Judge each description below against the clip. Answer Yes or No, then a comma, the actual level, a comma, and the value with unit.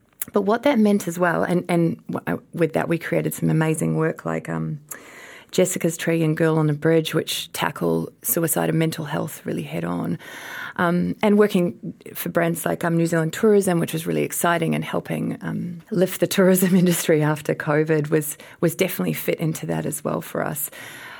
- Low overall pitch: No, medium, 170 Hz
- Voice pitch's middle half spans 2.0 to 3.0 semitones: Yes, average, 2.7 semitones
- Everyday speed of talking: Yes, average, 185 wpm